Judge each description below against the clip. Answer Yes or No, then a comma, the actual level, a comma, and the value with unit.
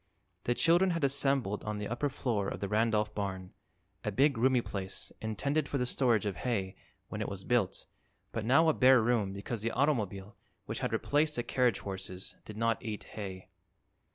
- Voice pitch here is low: Yes, low, 115 Hz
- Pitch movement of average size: Yes, average, 4.8 semitones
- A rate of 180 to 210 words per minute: Yes, average, 185 wpm